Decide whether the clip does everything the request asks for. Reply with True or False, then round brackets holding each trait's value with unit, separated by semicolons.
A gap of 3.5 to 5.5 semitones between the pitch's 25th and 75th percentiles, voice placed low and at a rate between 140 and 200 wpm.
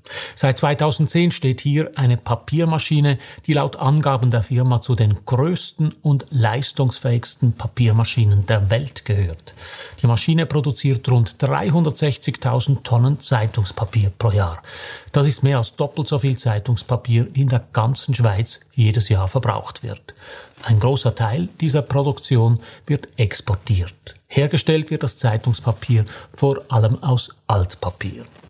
False (4.1 semitones; 125 Hz; 130 wpm)